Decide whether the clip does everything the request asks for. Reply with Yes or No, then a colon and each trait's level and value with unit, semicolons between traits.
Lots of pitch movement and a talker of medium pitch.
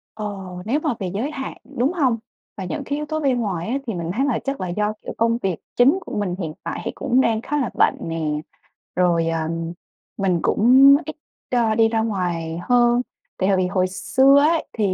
No: wide, 6.4 semitones; high, 220 Hz